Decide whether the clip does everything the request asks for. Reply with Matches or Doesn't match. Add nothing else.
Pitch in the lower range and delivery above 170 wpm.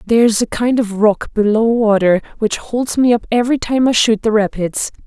Doesn't match